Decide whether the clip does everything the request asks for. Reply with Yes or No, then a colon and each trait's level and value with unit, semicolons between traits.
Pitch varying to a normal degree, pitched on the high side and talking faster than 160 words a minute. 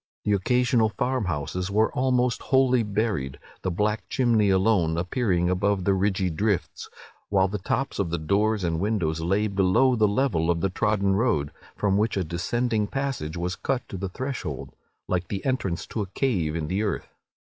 No: average, 4.0 semitones; low, 100 Hz; average, 180 wpm